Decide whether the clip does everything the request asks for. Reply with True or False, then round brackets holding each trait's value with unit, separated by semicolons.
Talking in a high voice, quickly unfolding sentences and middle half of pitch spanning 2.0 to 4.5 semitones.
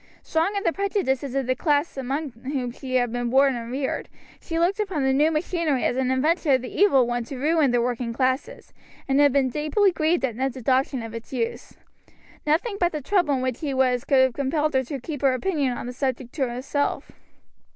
True (270 Hz; 220 wpm; 3.4 semitones)